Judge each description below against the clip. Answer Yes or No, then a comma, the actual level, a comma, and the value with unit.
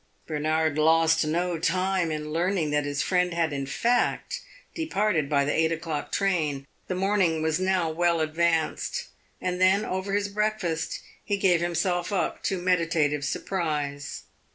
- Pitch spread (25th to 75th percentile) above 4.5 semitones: No, average, 3.1 semitones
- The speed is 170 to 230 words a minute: No, average, 150 wpm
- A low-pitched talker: No, medium, 170 Hz